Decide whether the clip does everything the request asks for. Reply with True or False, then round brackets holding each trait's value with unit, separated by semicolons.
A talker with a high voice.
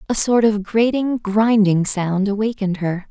True (210 Hz)